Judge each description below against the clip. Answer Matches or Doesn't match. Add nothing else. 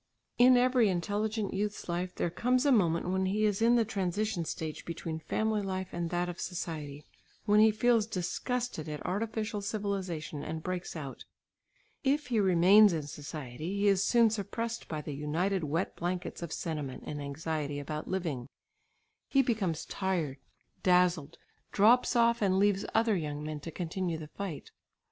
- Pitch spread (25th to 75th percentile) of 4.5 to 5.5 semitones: Matches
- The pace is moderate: Matches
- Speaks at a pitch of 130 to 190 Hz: Matches